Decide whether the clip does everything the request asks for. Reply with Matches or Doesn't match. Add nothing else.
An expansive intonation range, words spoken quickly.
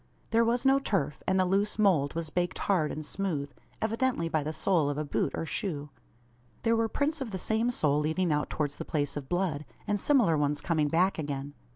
Matches